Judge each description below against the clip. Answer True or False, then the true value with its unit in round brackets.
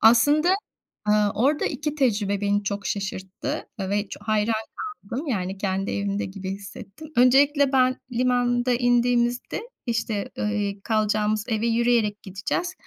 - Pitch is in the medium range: False (220 Hz)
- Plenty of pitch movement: False (3.5 semitones)